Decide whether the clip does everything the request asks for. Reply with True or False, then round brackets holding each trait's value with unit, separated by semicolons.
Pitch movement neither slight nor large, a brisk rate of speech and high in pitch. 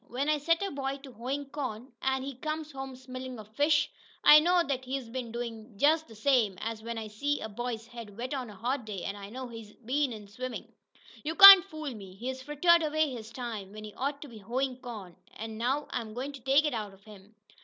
True (4.4 semitones; 230 wpm; 255 Hz)